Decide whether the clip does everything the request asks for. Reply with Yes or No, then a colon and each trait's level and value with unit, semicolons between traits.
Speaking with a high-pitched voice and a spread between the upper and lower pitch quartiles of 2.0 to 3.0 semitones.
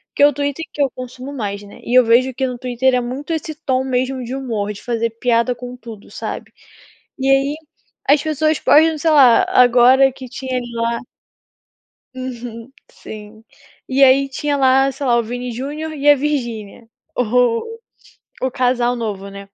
Yes: very high, 255 Hz; average, 2.7 semitones